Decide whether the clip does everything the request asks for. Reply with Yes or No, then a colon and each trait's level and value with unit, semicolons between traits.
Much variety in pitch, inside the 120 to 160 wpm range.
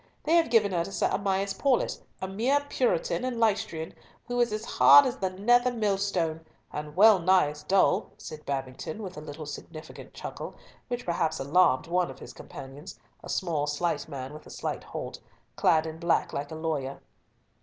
No: wide, 6.1 semitones; average, 180 wpm